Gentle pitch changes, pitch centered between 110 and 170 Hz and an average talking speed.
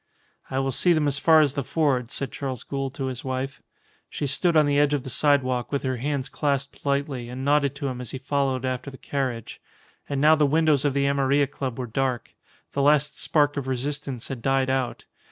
No: narrow, 1.7 semitones; medium, 140 Hz; fast, 220 wpm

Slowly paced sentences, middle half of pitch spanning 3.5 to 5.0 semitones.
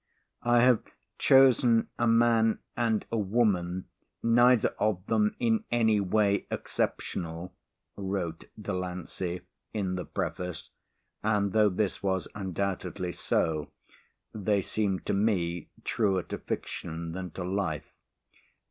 Yes: slow, 115 wpm; average, 3.8 semitones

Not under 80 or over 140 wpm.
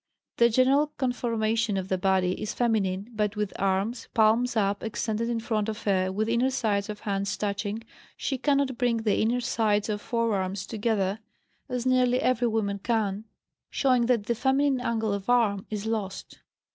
No: average, 170 wpm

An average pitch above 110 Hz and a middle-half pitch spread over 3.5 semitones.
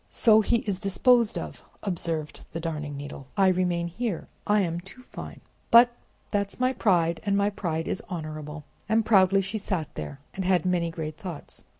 Yes: medium, 185 Hz; average, 3.9 semitones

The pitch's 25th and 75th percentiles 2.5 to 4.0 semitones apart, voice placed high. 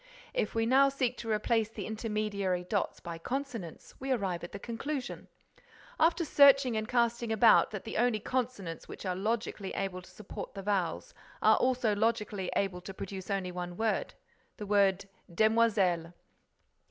Yes: average, 3.6 semitones; high, 215 Hz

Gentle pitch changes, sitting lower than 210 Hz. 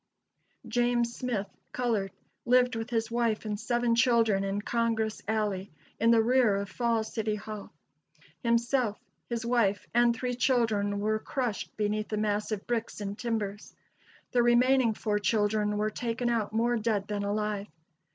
No: narrow, 2.3 semitones; high, 225 Hz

